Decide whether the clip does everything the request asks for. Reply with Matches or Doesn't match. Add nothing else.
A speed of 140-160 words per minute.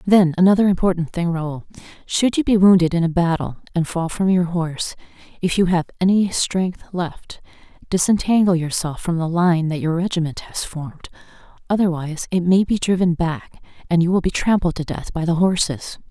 Doesn't match